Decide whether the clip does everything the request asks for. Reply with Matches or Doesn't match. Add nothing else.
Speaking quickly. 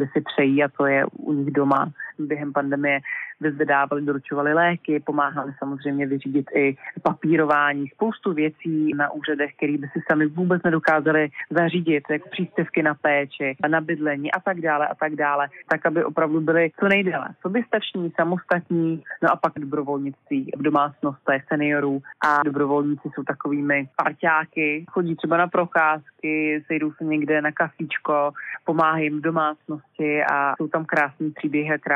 Doesn't match